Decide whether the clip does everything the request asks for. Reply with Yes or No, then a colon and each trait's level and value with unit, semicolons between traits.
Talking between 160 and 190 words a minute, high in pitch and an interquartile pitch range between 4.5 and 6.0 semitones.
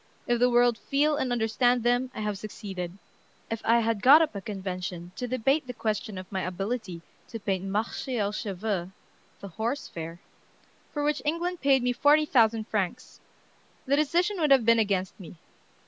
Yes: average, 180 wpm; high, 225 Hz; average, 4.9 semitones